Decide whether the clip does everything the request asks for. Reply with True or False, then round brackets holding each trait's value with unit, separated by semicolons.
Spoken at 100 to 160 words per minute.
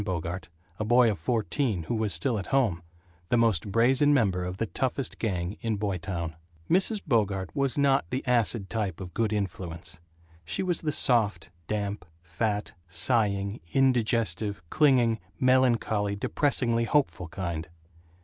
True (140 wpm)